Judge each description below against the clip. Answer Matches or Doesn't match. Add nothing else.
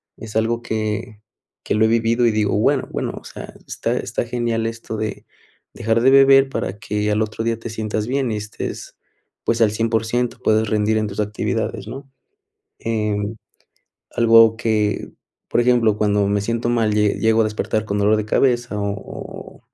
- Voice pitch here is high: Doesn't match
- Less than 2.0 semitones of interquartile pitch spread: Matches